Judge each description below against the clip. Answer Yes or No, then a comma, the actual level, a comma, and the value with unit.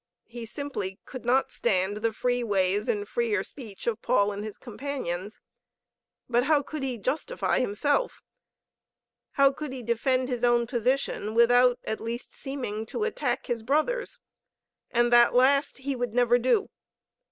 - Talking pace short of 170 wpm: Yes, average, 150 wpm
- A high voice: Yes, high, 240 Hz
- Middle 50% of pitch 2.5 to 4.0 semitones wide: Yes, average, 3.7 semitones